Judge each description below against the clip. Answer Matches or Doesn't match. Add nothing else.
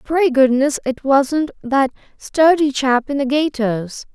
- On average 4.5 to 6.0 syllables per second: Doesn't match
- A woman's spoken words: Matches